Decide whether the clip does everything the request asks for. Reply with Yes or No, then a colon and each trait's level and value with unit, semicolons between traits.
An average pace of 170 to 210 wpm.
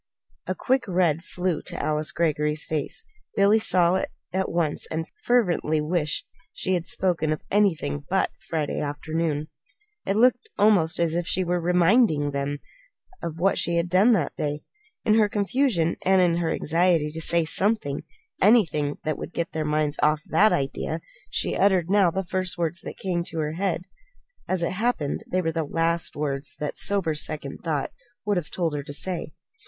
Yes: average, 180 wpm